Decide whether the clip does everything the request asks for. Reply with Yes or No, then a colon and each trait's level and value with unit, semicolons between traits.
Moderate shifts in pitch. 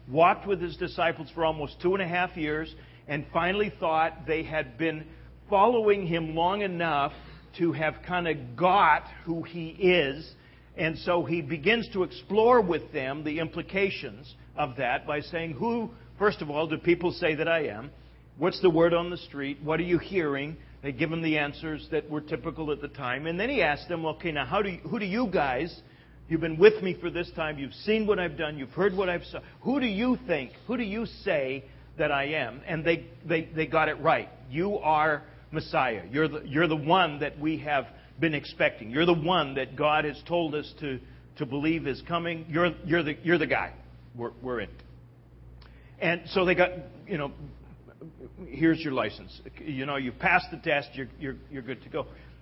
Yes: average, 3.3 semitones